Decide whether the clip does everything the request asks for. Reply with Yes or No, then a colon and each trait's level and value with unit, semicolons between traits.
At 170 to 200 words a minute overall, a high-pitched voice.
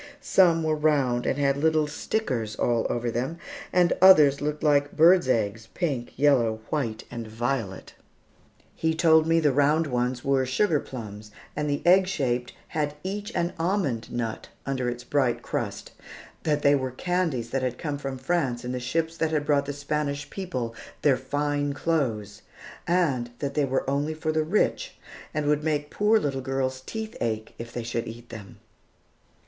No: average, 175 wpm; medium, 140 Hz